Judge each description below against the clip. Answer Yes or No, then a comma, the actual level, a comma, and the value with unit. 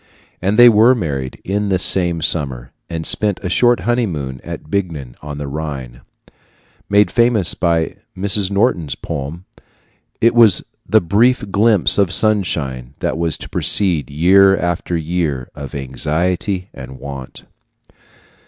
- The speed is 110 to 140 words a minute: Yes, slow, 135 wpm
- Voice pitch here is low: Yes, very low, 85 Hz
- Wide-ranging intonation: Yes, wide, 6.0 semitones